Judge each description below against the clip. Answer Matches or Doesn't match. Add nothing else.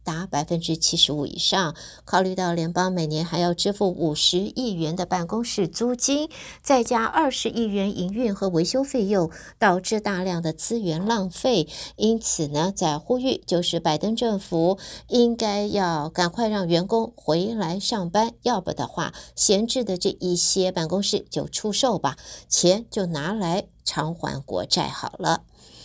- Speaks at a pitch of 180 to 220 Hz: Matches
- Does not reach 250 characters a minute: Matches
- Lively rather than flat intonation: Doesn't match